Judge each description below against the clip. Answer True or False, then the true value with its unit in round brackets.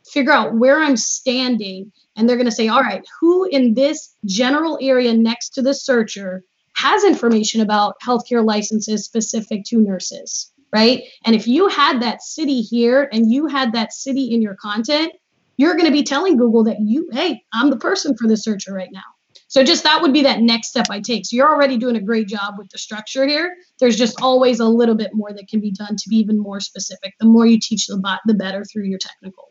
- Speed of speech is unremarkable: False (225 wpm)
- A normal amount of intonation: True (4.2 semitones)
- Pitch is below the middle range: False (235 Hz)